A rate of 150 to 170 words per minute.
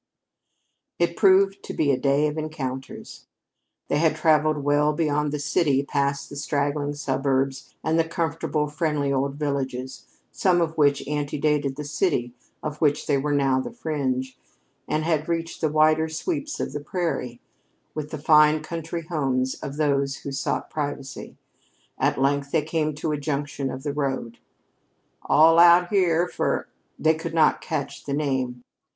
Yes: average, 160 wpm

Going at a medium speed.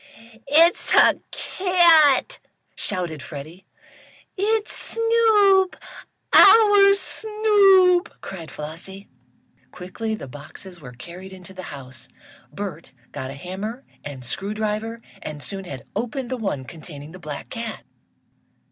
No: slow, 115 wpm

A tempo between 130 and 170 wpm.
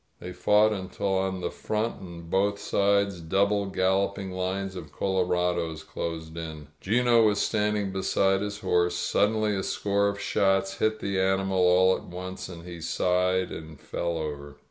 Yes: average, 165 wpm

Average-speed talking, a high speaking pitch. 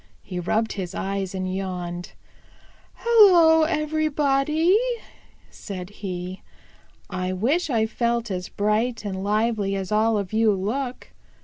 No: slow, 120 wpm; high, 215 Hz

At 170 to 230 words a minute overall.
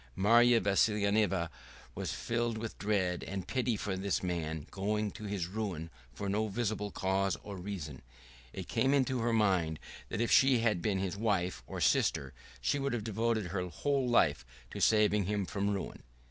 Yes: average, 175 wpm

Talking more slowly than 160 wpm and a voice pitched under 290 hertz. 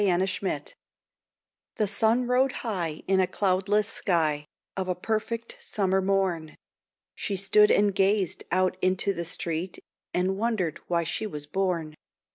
Yes: average, 140 wpm; high, 190 Hz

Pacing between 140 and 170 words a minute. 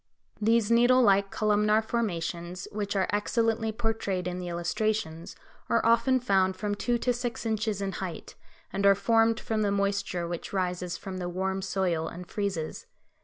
Yes: average, 165 wpm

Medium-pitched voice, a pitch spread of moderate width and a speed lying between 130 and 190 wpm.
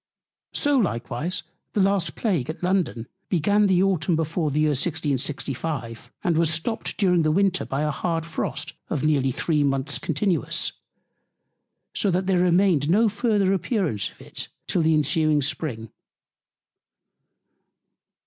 Yes: medium, 165 Hz; average, 4.4 semitones; average, 140 wpm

